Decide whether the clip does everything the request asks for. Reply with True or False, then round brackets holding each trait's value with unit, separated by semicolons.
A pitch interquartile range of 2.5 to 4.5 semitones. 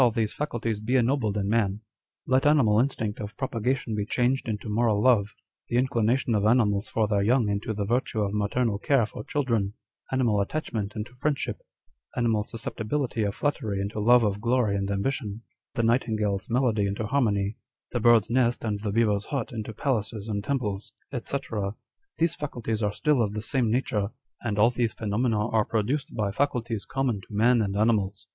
True (3.1 semitones)